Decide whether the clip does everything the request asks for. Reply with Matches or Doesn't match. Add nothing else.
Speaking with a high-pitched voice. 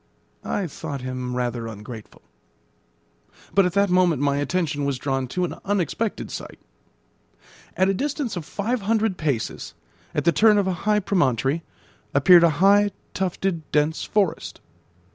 Doesn't match